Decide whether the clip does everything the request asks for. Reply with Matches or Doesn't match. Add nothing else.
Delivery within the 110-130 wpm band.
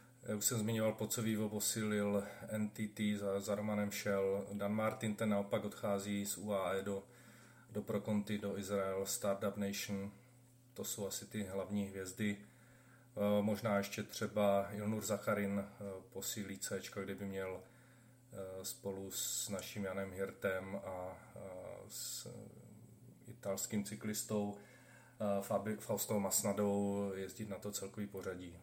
Matches